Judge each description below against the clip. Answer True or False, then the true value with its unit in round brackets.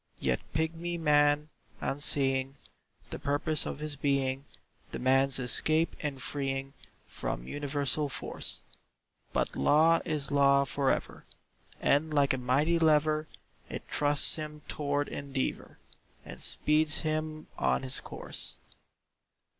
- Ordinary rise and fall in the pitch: False (2.1 semitones)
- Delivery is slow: True (115 wpm)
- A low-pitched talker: False (145 Hz)